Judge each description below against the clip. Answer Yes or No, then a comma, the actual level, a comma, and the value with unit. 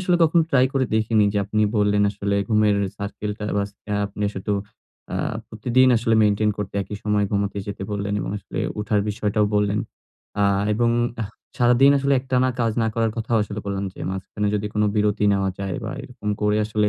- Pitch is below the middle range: Yes, low, 105 Hz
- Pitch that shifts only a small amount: Yes, narrow, 1.9 semitones